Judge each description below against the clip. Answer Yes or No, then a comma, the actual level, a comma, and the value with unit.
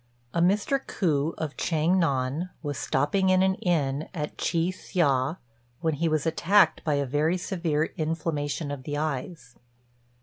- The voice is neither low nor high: Yes, medium, 160 Hz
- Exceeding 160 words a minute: No, average, 155 wpm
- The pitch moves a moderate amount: Yes, average, 3.4 semitones